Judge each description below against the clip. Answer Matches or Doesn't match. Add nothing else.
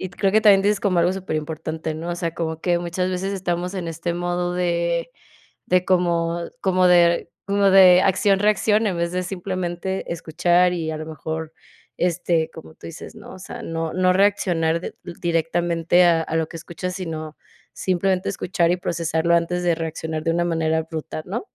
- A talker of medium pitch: Matches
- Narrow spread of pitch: Matches